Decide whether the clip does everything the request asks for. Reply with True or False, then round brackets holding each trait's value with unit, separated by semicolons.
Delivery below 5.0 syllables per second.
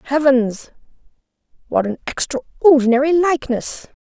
True (4.5 syllables/s)